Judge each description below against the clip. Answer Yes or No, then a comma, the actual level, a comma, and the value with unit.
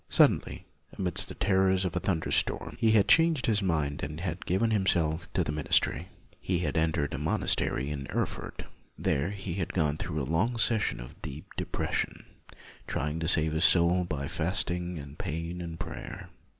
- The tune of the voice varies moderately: Yes, average, 3.7 semitones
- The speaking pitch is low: Yes, very low, 85 Hz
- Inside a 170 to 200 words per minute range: Yes, average, 175 wpm